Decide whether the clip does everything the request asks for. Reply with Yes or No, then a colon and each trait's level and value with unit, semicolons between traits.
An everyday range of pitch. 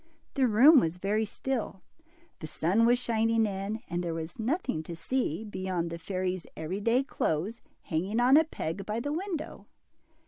No: wide, 5.8 semitones